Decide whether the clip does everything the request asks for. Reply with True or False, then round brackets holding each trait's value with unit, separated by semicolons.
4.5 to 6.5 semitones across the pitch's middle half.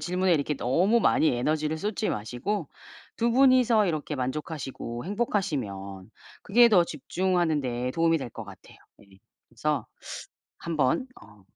False (7.3 semitones)